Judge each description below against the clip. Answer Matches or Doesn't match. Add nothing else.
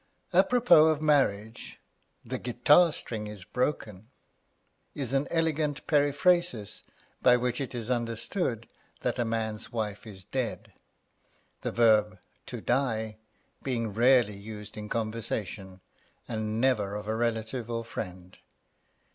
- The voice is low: Matches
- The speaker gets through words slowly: Matches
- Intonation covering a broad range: Doesn't match